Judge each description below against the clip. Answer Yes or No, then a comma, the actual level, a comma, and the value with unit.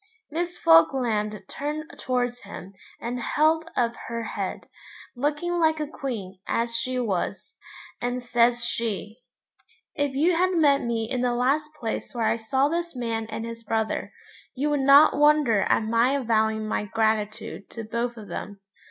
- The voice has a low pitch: No, high, 240 Hz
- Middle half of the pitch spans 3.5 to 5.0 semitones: Yes, average, 4.4 semitones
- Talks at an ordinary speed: Yes, average, 160 wpm